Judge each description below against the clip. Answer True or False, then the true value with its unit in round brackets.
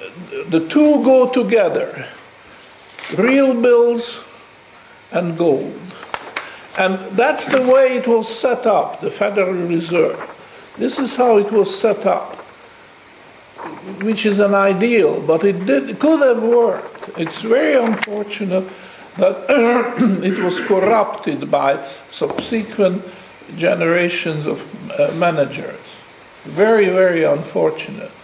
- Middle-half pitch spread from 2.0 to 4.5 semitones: False (4.9 semitones)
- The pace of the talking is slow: True (110 wpm)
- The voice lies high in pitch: True (210 Hz)